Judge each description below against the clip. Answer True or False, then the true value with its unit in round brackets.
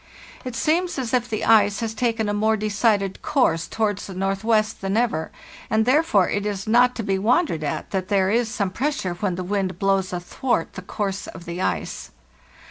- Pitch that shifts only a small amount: False (3.3 semitones)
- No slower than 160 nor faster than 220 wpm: True (195 wpm)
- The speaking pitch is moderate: False (205 Hz)